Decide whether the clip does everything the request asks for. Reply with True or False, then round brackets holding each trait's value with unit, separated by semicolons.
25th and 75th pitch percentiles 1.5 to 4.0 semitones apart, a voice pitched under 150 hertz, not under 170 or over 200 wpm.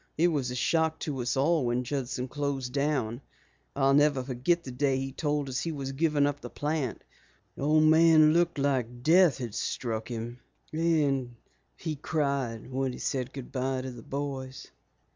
True (3.1 semitones; 135 Hz; 180 wpm)